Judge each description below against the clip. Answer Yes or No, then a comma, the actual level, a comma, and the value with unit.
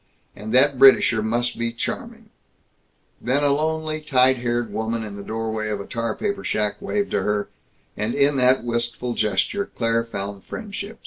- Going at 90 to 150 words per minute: No, average, 170 wpm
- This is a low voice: Yes, low, 120 Hz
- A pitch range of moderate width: Yes, average, 4.2 semitones